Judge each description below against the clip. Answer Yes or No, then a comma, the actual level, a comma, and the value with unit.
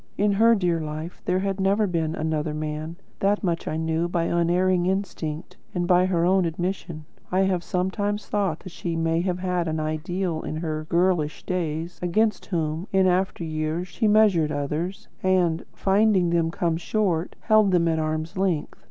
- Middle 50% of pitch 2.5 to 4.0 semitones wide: Yes, average, 2.9 semitones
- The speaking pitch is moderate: Yes, medium, 175 Hz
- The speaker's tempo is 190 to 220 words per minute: No, average, 175 wpm